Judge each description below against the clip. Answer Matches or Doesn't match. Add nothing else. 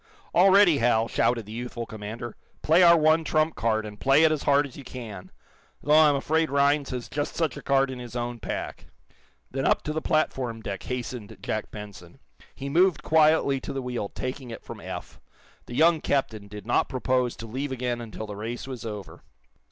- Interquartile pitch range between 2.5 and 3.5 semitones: Doesn't match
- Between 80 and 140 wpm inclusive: Doesn't match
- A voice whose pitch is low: Matches